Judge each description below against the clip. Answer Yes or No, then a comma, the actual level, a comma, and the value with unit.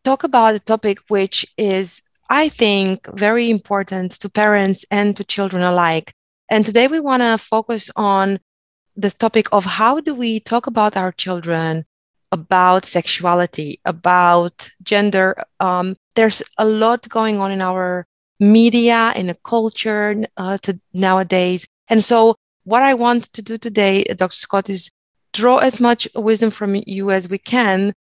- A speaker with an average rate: Yes, average, 155 wpm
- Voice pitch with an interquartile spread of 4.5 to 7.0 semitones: No, average, 3.2 semitones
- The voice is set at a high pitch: Yes, high, 205 Hz